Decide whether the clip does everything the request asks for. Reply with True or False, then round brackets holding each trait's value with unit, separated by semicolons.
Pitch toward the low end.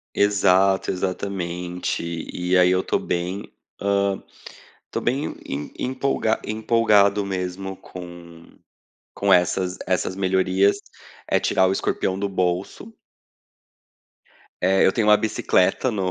True (95 Hz)